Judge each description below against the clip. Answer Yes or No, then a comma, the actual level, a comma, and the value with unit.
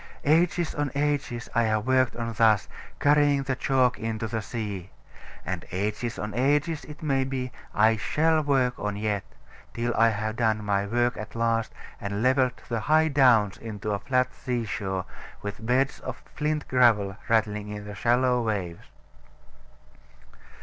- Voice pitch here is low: Yes, low, 115 Hz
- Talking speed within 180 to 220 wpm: No, average, 155 wpm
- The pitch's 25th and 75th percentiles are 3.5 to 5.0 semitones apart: Yes, average, 4.0 semitones